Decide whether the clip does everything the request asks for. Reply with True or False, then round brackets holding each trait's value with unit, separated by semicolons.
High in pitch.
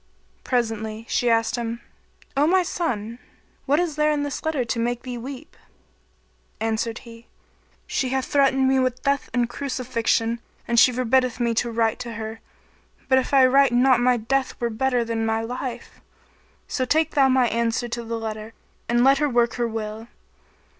True (240 Hz)